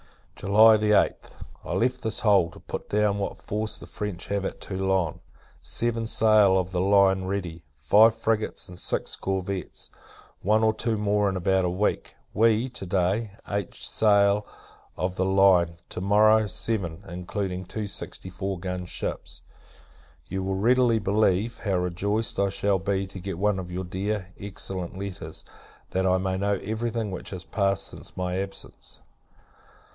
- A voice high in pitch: No, low, 100 Hz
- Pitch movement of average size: No, narrow, 2.2 semitones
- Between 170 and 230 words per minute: No, average, 160 wpm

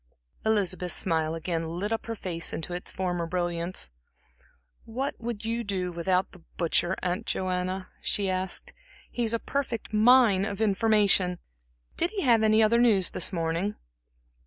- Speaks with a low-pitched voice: No, high, 190 Hz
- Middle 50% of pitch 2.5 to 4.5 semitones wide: Yes, average, 3.9 semitones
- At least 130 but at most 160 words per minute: Yes, average, 150 wpm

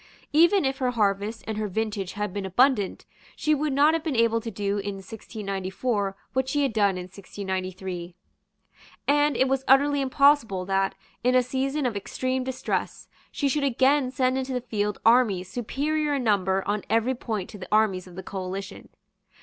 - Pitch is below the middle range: No, high, 225 Hz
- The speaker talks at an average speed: Yes, average, 180 wpm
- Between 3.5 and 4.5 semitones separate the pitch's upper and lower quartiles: No, average, 5.3 semitones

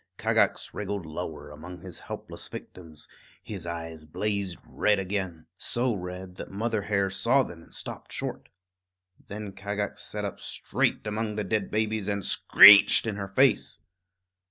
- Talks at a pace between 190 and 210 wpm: No, average, 150 wpm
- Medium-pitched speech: No, low, 100 Hz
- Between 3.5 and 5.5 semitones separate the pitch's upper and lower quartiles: No, average, 3.0 semitones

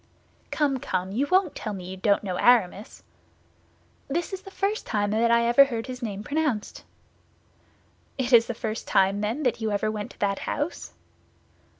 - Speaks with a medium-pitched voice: No, high, 230 Hz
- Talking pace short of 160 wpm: No, average, 175 wpm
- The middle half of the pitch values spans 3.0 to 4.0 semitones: No, average, 5.2 semitones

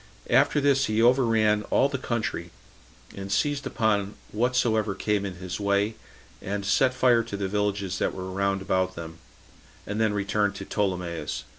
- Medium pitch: No, low, 105 Hz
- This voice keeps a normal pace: Yes, average, 160 wpm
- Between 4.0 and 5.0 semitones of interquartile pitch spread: No, average, 3.1 semitones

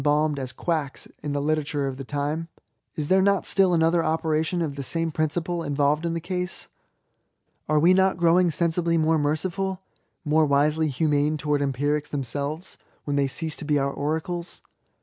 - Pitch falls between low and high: Yes, medium, 155 Hz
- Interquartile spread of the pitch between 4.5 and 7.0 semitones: No, narrow, 2.5 semitones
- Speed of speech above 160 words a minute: Yes, average, 170 wpm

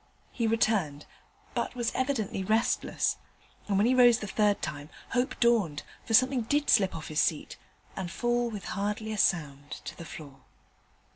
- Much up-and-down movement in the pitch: Yes, wide, 5.7 semitones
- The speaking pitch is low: No, high, 215 Hz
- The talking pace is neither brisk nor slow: Yes, average, 165 wpm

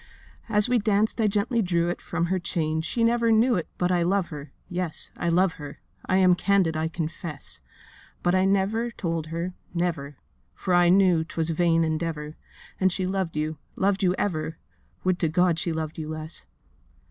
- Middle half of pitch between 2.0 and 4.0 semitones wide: Yes, average, 3.1 semitones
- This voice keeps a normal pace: Yes, average, 175 wpm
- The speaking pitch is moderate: Yes, medium, 175 Hz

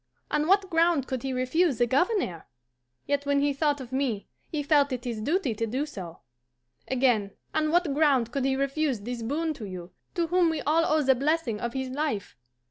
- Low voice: No, very high, 275 Hz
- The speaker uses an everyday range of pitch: Yes, average, 4.3 semitones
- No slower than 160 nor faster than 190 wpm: No, fast, 205 wpm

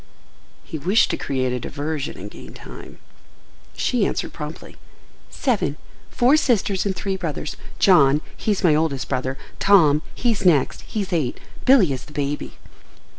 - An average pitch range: No, wide, 6.0 semitones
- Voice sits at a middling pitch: Yes, medium, 160 Hz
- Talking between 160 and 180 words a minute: No, average, 140 wpm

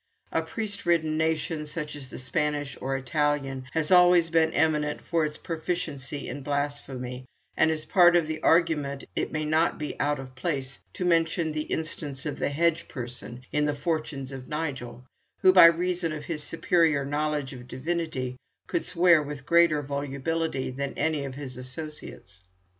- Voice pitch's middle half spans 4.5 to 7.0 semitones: No, average, 3.1 semitones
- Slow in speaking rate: No, average, 170 wpm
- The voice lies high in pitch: No, medium, 150 Hz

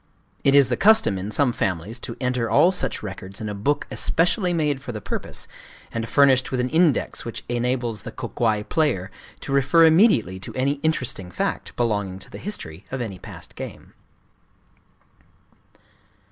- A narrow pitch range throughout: No, wide, 5.5 semitones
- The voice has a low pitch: Yes, low, 125 Hz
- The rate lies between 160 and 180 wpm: Yes, average, 170 wpm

